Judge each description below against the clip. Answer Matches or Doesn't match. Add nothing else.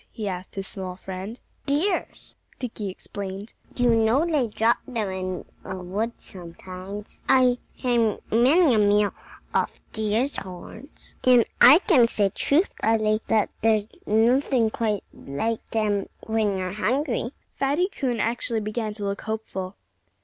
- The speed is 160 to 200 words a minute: Doesn't match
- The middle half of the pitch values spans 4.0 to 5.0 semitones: Doesn't match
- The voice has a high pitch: Matches